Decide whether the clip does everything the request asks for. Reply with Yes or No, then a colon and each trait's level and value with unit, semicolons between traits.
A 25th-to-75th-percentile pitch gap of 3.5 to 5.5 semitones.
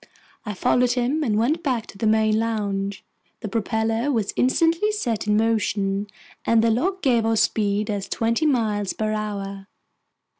No: average, 2.7 semitones